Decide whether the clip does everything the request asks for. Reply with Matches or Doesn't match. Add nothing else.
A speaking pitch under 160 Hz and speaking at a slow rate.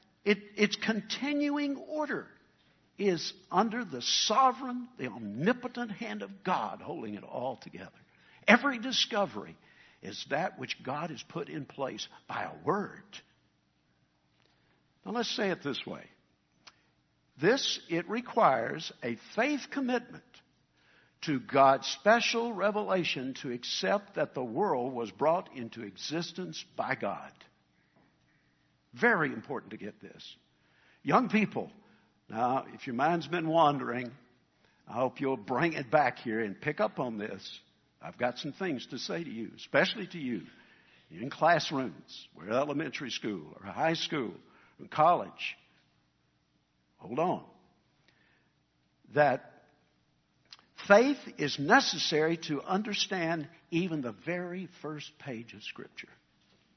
Doesn't match